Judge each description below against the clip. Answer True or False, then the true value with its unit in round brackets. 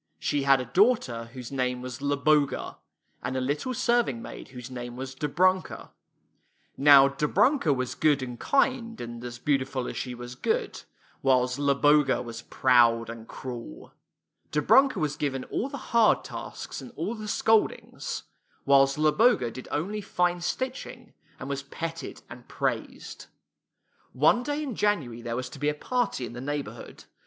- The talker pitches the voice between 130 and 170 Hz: True (140 Hz)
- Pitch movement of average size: False (6.7 semitones)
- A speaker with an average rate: True (155 wpm)